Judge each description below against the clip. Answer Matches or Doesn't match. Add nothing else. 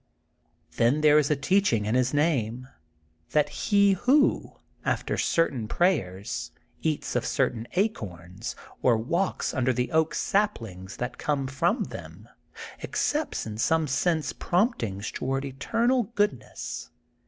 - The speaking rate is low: Matches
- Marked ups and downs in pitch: Matches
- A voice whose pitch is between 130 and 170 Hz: Matches